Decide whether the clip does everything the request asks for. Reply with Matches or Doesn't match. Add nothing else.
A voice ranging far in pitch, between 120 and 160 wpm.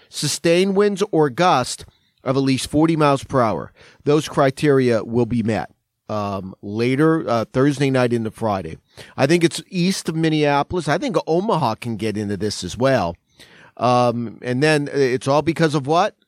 Doesn't match